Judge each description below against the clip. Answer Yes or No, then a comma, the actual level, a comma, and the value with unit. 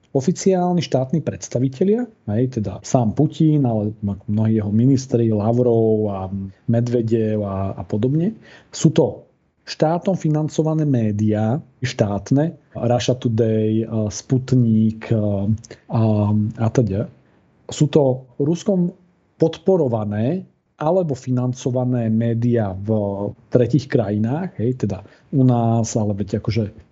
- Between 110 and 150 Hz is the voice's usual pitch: Yes, low, 120 Hz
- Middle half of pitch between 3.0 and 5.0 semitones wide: Yes, average, 4.6 semitones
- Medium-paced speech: No, slow, 100 wpm